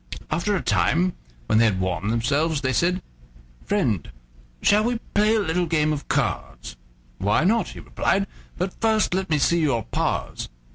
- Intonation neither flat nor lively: No, wide, 8.4 semitones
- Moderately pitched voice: Yes, medium, 165 Hz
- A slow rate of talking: No, average, 170 wpm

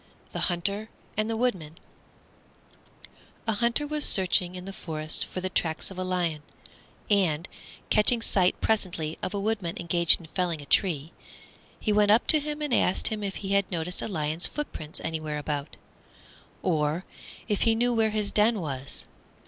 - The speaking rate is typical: Yes, average, 170 wpm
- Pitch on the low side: No, medium, 185 Hz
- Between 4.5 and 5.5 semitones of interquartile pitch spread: Yes, average, 4.9 semitones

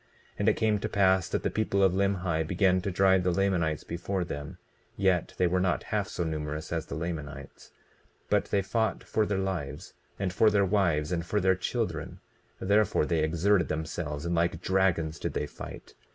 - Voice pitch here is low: Yes, very low, 90 Hz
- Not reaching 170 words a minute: No, average, 195 wpm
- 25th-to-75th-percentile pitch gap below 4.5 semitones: Yes, average, 3.3 semitones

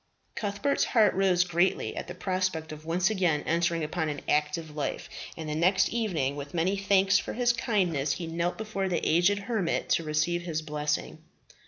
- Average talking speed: Yes, average, 180 wpm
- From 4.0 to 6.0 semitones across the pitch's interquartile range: No, average, 3.6 semitones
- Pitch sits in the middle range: Yes, medium, 175 Hz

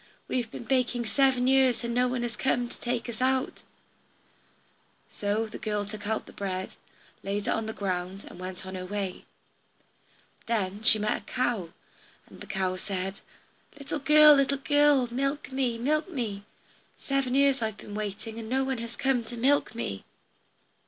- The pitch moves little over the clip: No, average, 4.5 semitones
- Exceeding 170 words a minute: Yes, average, 180 wpm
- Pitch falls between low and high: No, high, 235 Hz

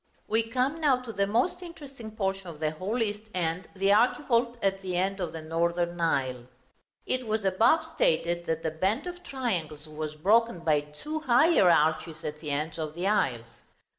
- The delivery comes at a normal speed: Yes, average, 185 wpm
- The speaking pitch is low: No, high, 190 Hz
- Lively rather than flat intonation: Yes, wide, 6.6 semitones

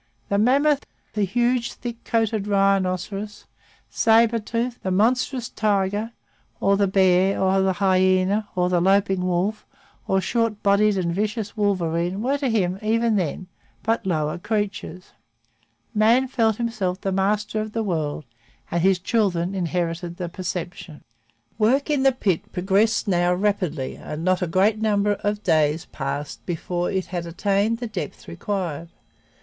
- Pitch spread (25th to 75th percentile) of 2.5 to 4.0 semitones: Yes, average, 3.4 semitones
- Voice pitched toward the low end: No, high, 195 Hz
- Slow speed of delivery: No, average, 145 wpm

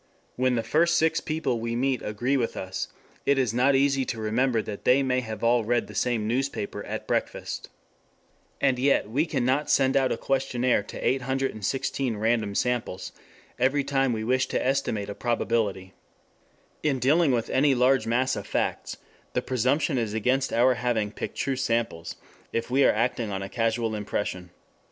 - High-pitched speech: No, low, 125 Hz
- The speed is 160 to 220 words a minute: Yes, average, 175 wpm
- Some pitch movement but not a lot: Yes, average, 3.2 semitones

